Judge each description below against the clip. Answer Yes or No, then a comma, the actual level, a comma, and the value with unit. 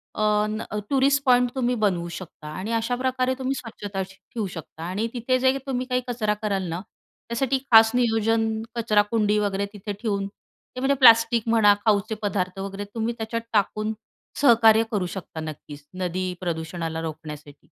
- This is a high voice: Yes, high, 215 Hz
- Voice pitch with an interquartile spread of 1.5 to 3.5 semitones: No, average, 4.0 semitones